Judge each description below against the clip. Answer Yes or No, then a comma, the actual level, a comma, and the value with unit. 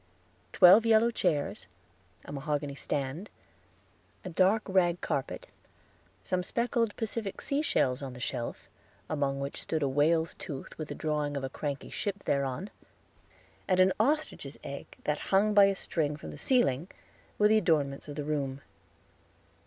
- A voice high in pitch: No, medium, 155 Hz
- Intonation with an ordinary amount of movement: No, wide, 6.0 semitones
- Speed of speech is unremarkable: Yes, average, 155 wpm